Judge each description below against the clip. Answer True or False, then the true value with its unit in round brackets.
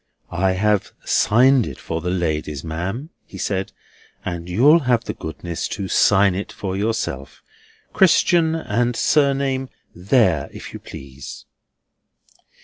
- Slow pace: True (130 wpm)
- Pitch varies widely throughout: True (6.6 semitones)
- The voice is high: False (100 Hz)